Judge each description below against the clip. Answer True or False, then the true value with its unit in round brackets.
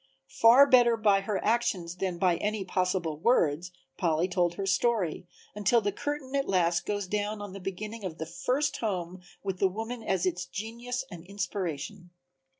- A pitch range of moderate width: True (4.0 semitones)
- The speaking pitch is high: True (195 Hz)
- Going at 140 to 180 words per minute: True (170 wpm)